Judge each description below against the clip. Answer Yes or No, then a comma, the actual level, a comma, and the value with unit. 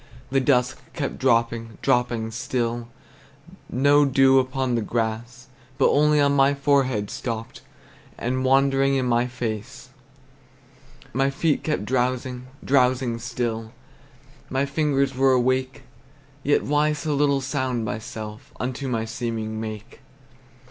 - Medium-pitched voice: No, low, 130 Hz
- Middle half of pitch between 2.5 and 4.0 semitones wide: Yes, average, 2.8 semitones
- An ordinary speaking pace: No, slow, 120 wpm